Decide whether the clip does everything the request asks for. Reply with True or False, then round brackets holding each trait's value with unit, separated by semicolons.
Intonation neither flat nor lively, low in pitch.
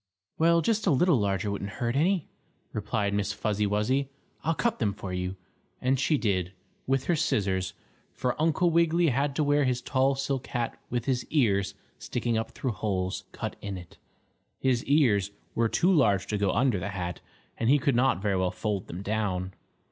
False (5.8 semitones; 115 Hz)